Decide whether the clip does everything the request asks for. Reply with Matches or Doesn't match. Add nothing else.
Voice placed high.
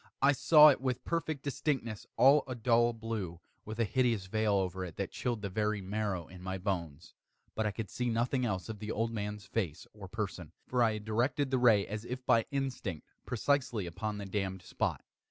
Doesn't match